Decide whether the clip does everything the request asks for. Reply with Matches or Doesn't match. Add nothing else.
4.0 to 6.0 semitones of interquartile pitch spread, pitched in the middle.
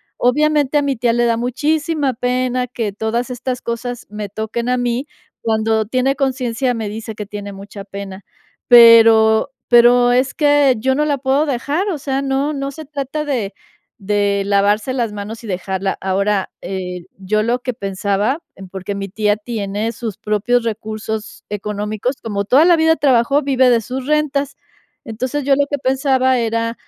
Doesn't match